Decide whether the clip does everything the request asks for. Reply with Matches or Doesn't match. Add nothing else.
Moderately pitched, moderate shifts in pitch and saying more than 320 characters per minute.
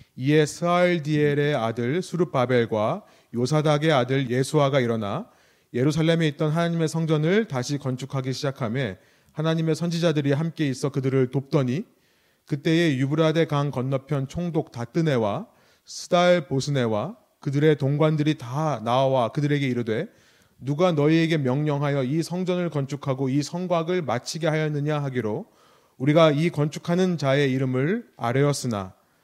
Matches